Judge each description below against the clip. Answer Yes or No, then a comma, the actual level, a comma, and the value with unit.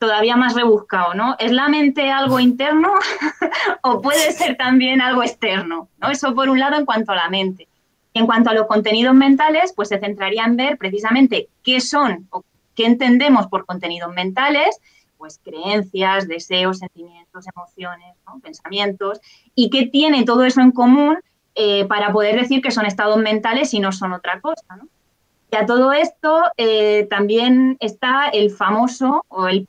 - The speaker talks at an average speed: Yes, average, 170 wpm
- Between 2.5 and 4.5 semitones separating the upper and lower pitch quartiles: No, wide, 5.4 semitones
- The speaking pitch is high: Yes, high, 230 Hz